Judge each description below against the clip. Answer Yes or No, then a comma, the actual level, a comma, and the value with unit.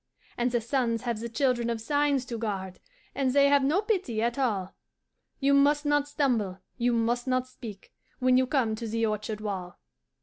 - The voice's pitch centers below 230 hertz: No, high, 240 Hz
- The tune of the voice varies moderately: Yes, average, 3.7 semitones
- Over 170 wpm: Yes, average, 190 wpm